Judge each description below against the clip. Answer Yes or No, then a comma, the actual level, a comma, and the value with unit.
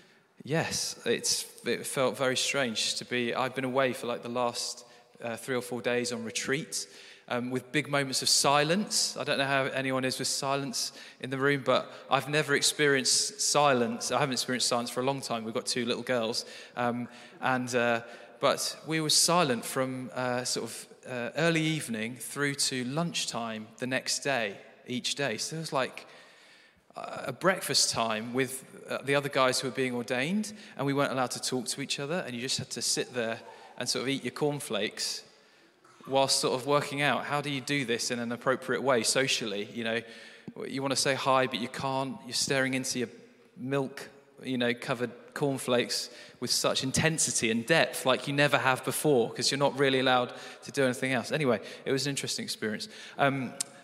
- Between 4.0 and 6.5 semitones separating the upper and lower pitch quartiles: No, narrow, 2.4 semitones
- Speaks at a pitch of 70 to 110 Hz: No, low, 130 Hz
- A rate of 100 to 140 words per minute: No, average, 195 wpm